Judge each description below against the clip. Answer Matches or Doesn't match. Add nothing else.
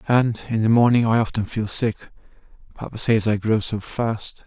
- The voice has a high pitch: Doesn't match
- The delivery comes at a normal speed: Matches